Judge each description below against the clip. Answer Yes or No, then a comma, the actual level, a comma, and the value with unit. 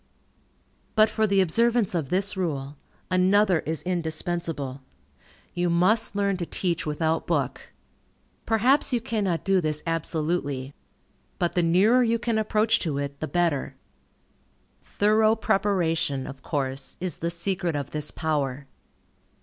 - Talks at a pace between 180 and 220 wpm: No, slow, 135 wpm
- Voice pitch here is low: No, medium, 175 Hz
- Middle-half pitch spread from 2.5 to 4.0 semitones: No, average, 4.8 semitones